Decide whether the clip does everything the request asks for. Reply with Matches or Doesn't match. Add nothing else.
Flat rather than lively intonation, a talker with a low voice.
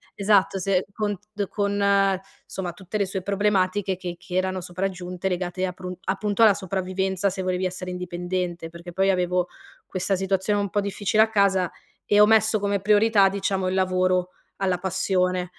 Doesn't match